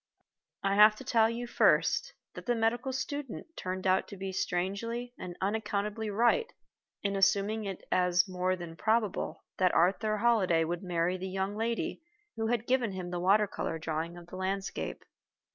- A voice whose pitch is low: No, high, 200 Hz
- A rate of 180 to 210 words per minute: No, average, 170 wpm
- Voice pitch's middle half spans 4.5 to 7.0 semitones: No, average, 3.6 semitones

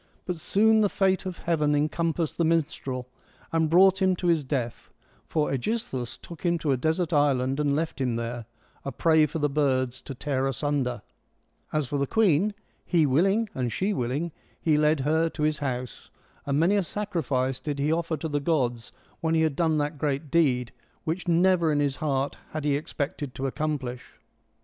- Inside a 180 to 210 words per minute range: Yes, average, 190 wpm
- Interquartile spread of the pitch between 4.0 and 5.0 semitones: No, average, 3.6 semitones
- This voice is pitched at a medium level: Yes, medium, 150 Hz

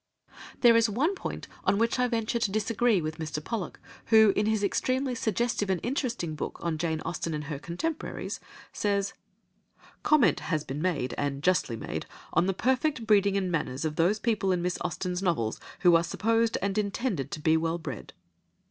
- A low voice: No, high, 195 Hz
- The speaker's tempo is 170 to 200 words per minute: Yes, average, 185 wpm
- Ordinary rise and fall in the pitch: No, wide, 5.9 semitones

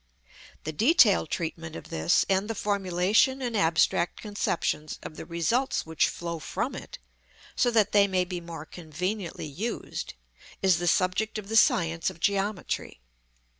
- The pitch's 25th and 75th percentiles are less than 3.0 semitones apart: No, average, 4.1 semitones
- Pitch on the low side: No, medium, 180 Hz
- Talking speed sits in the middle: Yes, average, 150 wpm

